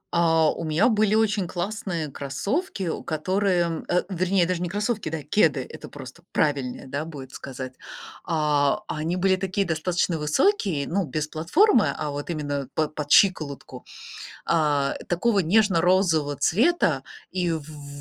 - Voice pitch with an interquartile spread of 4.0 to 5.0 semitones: Yes, average, 4.4 semitones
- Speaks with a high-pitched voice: No, medium, 165 Hz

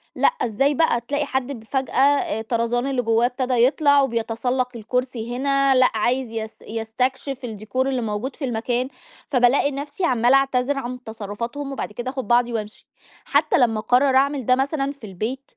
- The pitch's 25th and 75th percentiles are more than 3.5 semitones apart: No, average, 2.8 semitones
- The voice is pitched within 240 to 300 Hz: Yes, very high, 250 Hz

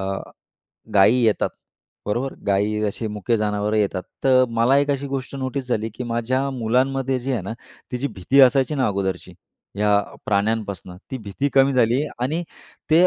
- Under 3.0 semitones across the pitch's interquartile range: No, average, 4.3 semitones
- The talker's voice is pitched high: No, low, 120 Hz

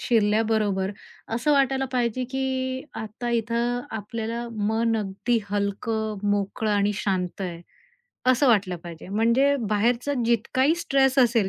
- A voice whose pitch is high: Yes, high, 230 Hz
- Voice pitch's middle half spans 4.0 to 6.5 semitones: No, average, 3.6 semitones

